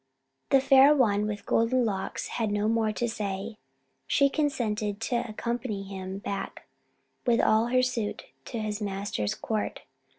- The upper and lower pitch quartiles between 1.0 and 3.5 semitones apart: Yes, average, 2.9 semitones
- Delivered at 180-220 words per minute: No, average, 145 wpm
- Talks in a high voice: Yes, high, 220 Hz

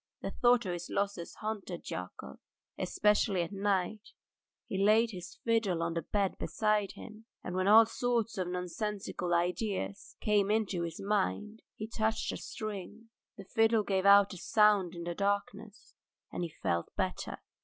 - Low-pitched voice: No, high, 200 Hz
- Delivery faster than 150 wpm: Yes, average, 160 wpm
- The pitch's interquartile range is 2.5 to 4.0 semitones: Yes, average, 3.2 semitones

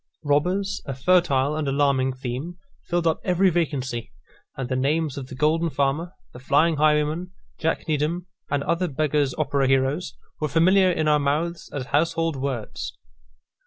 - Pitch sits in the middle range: Yes, medium, 150 Hz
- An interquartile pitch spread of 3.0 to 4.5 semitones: Yes, average, 3.6 semitones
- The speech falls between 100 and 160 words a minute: Yes, average, 155 wpm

